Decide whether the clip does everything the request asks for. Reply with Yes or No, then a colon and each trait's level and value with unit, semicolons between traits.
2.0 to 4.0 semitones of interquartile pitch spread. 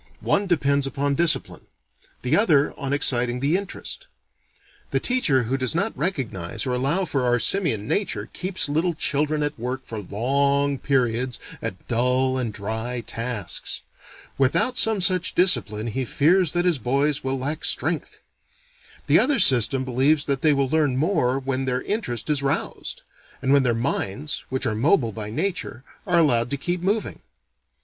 No: average, 4.4 semitones